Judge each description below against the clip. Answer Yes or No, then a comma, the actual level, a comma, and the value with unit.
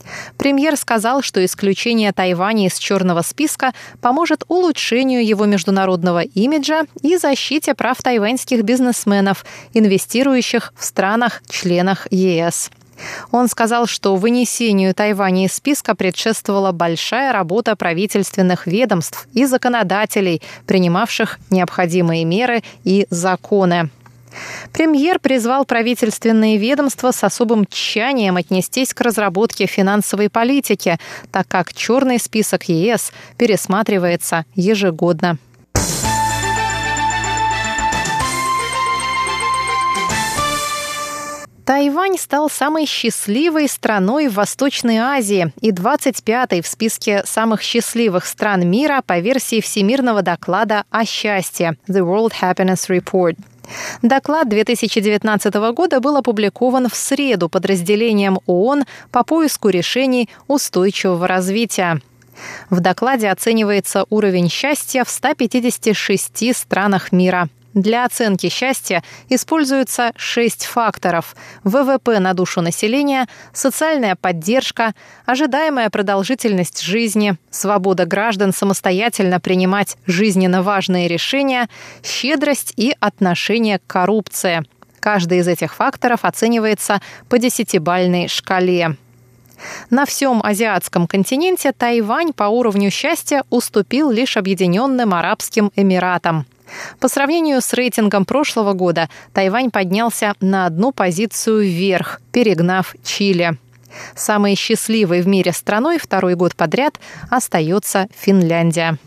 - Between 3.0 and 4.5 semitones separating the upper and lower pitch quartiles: No, average, 5.1 semitones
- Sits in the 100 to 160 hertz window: No, high, 210 Hz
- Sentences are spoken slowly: Yes, slow, 100 wpm